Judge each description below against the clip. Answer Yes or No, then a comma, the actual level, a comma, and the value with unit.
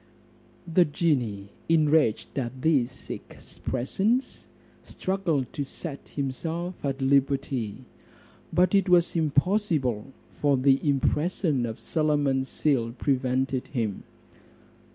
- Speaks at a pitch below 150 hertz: Yes, medium, 140 Hz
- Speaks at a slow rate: Yes, slow, 95 wpm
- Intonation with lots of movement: No, average, 4.1 semitones